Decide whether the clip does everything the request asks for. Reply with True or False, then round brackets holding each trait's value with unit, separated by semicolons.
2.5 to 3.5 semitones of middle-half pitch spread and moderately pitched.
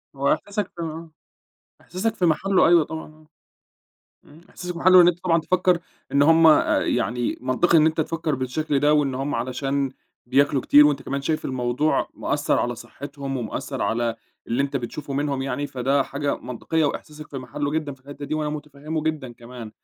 True (3.0 semitones; 145 Hz)